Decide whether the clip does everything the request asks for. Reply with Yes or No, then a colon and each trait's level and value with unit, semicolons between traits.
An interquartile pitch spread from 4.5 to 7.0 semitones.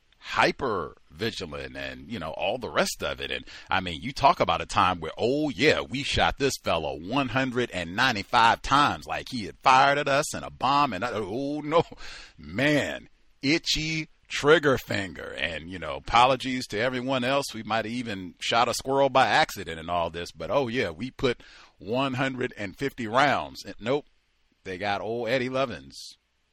Yes: average, 4.8 semitones